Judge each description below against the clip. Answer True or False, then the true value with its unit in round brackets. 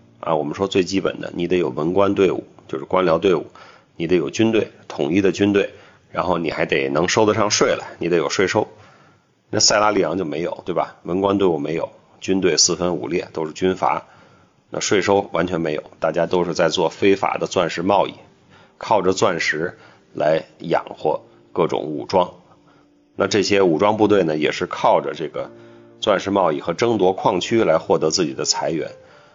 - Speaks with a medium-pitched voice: False (95 Hz)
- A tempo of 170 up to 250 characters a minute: False (275 characters per minute)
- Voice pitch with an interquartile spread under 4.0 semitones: True (3.4 semitones)